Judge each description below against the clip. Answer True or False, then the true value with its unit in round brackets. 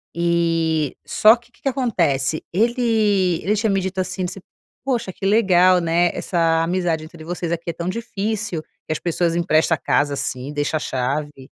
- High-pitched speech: False (175 Hz)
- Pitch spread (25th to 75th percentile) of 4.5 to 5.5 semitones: False (3.9 semitones)